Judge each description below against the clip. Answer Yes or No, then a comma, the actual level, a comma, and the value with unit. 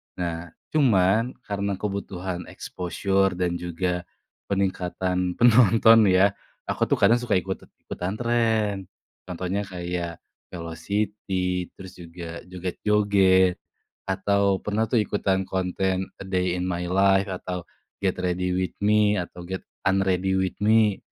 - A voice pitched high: No, very low, 95 Hz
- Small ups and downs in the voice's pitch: Yes, narrow, 2.0 semitones